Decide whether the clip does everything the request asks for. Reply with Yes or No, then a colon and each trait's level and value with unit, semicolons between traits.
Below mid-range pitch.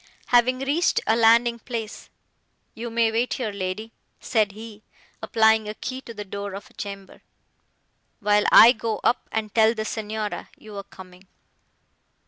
No: high, 220 Hz